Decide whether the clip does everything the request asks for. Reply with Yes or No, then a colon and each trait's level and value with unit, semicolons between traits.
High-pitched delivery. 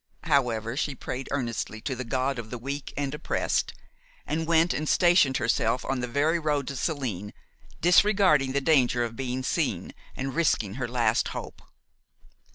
No: low, 135 Hz